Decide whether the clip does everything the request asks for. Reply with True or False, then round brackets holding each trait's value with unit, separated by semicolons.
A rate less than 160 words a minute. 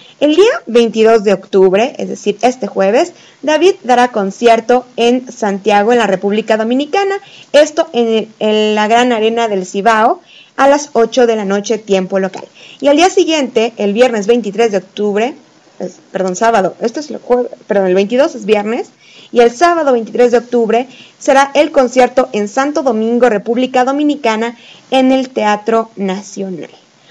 False (165 wpm)